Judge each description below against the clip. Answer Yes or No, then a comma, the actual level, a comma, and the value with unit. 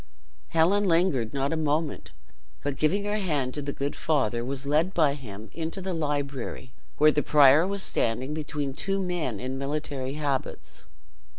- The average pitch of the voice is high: No, medium, 145 Hz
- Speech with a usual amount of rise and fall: Yes, average, 3.4 semitones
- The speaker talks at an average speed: Yes, average, 165 wpm